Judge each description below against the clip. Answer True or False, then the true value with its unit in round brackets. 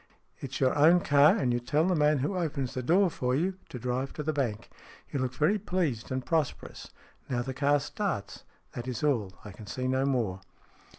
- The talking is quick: True (220 wpm)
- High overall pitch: False (135 Hz)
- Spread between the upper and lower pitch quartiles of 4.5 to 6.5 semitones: False (3.5 semitones)